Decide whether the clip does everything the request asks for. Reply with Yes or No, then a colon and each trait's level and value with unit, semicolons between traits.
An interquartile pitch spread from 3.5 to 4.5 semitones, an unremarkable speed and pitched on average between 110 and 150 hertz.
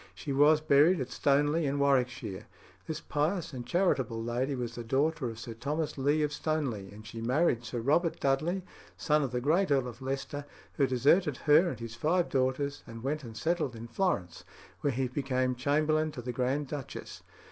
Yes: average, 3.8 semitones; average, 190 wpm; medium, 140 Hz